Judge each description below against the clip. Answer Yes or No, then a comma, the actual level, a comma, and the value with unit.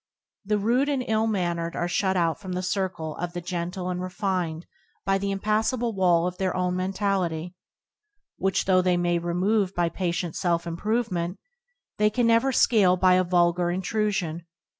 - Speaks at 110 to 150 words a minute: No, average, 165 wpm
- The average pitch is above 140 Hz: Yes, medium, 185 Hz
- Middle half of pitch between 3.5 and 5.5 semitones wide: No, average, 2.8 semitones